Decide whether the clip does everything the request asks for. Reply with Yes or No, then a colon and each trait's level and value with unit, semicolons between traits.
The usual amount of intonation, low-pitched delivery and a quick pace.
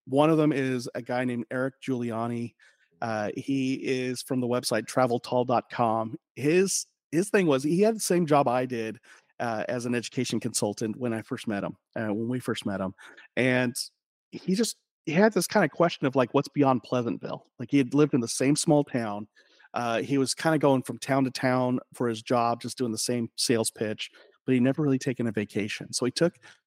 Yes: average, 3.3 semitones; low, 125 Hz; fast, 215 wpm